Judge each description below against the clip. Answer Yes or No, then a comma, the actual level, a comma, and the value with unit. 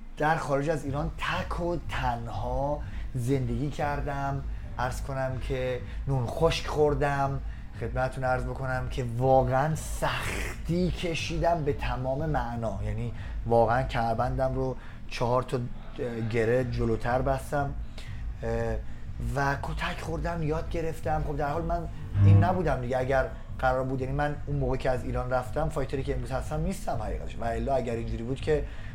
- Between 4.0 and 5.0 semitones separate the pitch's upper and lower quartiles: No, average, 3.5 semitones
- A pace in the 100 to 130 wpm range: No, average, 145 wpm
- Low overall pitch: Yes, low, 130 Hz